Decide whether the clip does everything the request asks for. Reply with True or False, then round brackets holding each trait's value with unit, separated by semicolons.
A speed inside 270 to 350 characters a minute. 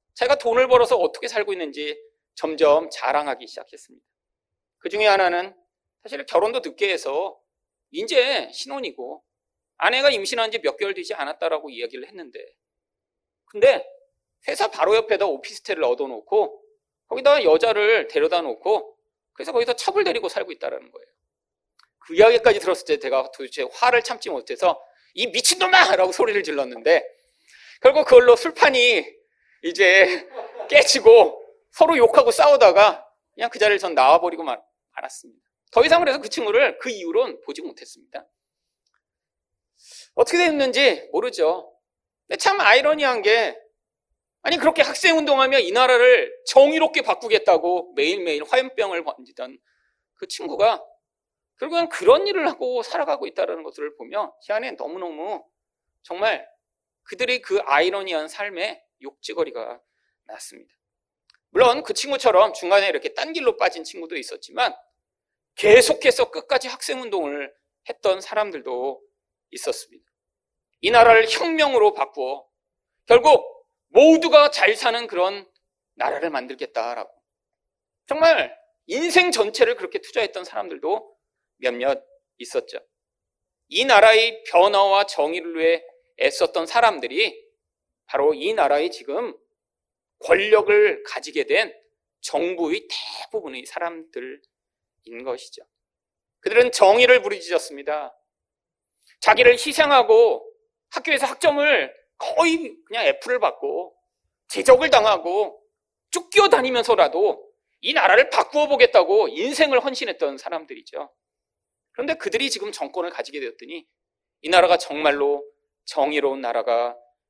True (295 characters per minute)